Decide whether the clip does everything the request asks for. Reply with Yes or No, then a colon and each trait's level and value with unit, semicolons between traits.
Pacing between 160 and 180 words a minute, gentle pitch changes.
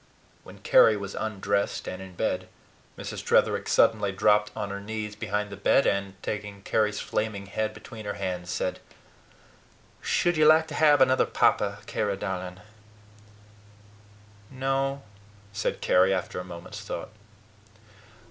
No: average, 140 wpm; narrow, 2.3 semitones